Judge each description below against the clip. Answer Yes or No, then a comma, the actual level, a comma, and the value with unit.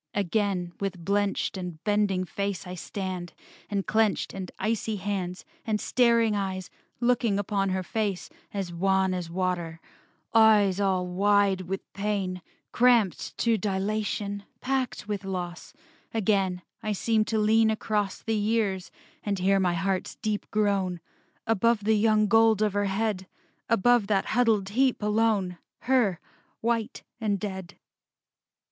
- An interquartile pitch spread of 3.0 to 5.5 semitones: No, narrow, 2.5 semitones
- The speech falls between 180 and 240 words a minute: No, slow, 135 wpm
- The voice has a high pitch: Yes, high, 200 Hz